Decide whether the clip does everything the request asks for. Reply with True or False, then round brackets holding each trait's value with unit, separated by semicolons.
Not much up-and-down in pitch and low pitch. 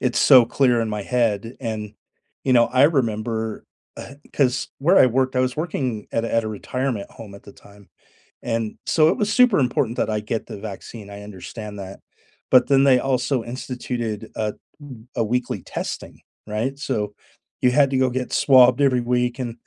False (3.2 semitones; 120 Hz)